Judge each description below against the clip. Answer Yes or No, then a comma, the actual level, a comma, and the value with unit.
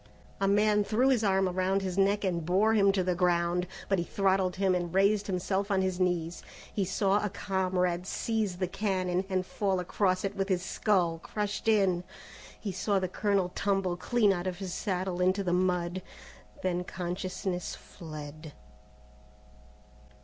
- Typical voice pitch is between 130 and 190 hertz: Yes, medium, 185 Hz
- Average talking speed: Yes, average, 165 wpm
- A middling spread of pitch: No, narrow, 1.8 semitones